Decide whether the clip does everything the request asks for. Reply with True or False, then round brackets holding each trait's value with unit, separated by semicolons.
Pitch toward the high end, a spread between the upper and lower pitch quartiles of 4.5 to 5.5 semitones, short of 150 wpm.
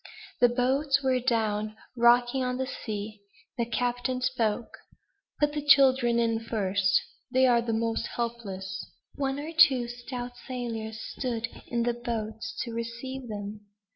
False (240 Hz; 2.4 semitones; 140 wpm)